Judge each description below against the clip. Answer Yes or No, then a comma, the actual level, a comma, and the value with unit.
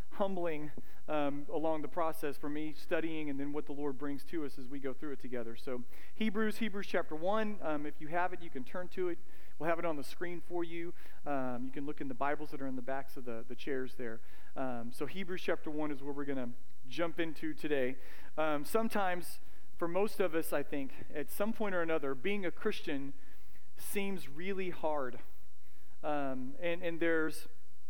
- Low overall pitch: No, medium, 150 Hz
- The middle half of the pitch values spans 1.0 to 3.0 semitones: No, average, 4.2 semitones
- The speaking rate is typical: No, fast, 210 wpm